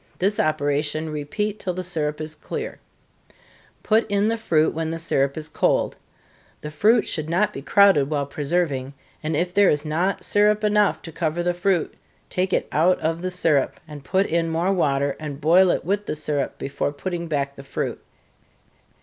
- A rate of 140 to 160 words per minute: No, average, 185 wpm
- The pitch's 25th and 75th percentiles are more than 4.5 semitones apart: No, average, 3.9 semitones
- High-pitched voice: No, medium, 165 Hz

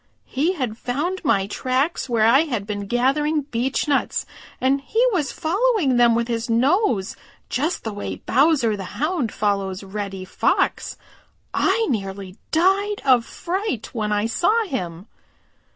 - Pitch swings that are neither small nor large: No, wide, 7.2 semitones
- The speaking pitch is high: Yes, very high, 255 Hz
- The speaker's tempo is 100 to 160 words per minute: Yes, average, 140 wpm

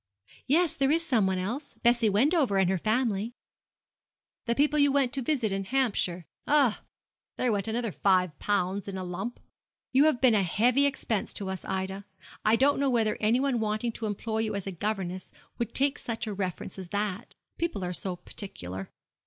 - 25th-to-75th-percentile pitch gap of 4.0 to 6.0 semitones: Yes, average, 5.1 semitones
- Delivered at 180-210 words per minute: Yes, average, 185 wpm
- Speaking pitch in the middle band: No, high, 220 Hz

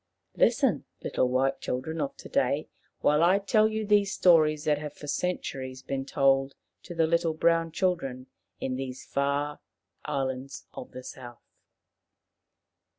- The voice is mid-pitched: Yes, medium, 150 Hz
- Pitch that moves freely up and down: No, average, 3.9 semitones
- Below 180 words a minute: Yes, average, 145 wpm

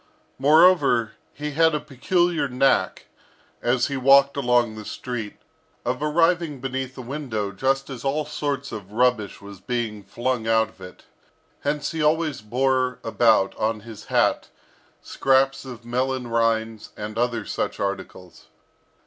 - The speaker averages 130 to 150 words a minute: Yes, average, 140 wpm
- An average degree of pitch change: Yes, average, 3.8 semitones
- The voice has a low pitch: Yes, low, 125 Hz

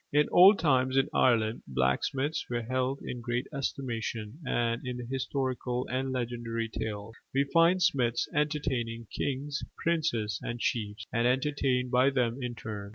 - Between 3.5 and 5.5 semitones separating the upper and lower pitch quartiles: No, average, 2.9 semitones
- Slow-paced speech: No, average, 150 wpm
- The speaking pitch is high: No, low, 125 Hz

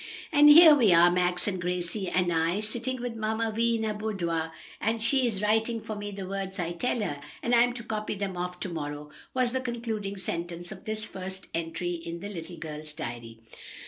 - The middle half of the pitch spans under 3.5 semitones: No, average, 4.5 semitones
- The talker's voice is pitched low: No, high, 195 Hz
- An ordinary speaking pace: No, fast, 210 wpm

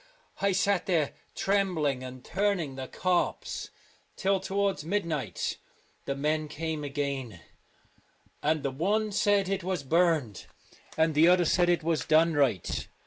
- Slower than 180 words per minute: Yes, average, 140 wpm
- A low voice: No, medium, 160 Hz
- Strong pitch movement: No, average, 4.9 semitones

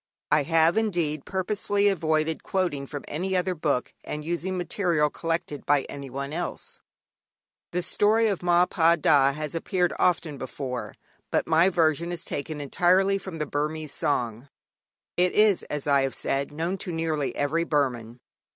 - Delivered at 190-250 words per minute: No, average, 155 wpm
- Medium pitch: Yes, medium, 160 Hz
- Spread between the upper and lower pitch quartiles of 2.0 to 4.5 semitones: Yes, average, 3.7 semitones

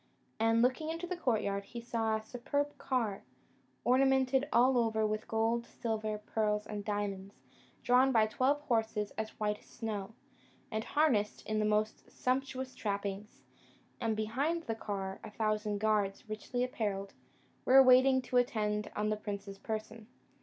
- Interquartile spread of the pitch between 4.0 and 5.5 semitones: No, average, 3.2 semitones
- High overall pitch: Yes, high, 220 Hz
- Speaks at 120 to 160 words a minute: Yes, average, 150 wpm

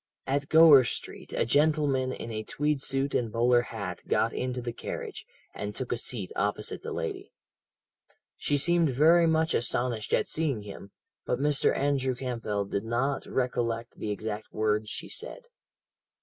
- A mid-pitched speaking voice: No, low, 125 Hz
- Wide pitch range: No, average, 4.3 semitones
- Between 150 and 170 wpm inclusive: Yes, average, 160 wpm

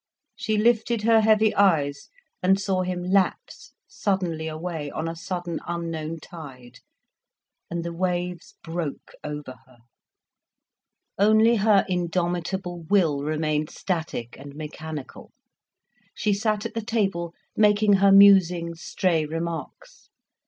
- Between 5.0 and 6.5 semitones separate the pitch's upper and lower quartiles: No, average, 3.9 semitones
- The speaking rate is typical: No, slow, 115 wpm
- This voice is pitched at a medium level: Yes, medium, 175 Hz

